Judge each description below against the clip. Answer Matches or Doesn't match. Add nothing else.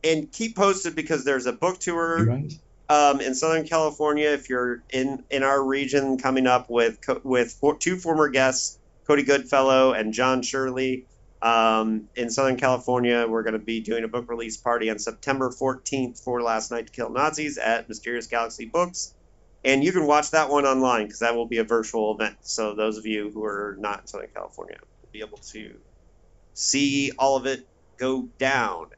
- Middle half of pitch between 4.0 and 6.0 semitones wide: Doesn't match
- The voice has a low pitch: Matches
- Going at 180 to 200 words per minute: Matches